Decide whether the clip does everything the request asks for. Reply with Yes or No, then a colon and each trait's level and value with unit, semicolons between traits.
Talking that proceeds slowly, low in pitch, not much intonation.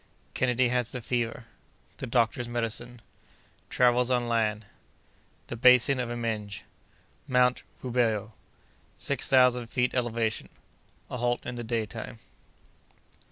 Yes: slow, 85 wpm; low, 120 Hz; narrow, 1.6 semitones